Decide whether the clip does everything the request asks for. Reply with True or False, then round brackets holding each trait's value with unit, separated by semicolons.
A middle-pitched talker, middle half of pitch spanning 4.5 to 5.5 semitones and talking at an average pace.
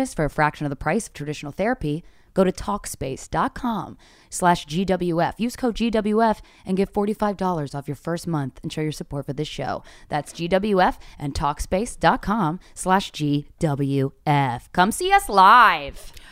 True (170 Hz; 5.0 semitones; 150 wpm)